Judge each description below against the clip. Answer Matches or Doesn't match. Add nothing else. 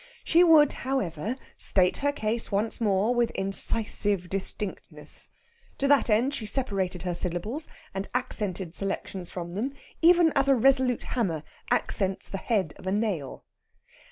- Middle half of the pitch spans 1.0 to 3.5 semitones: Doesn't match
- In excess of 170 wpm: Doesn't match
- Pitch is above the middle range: Matches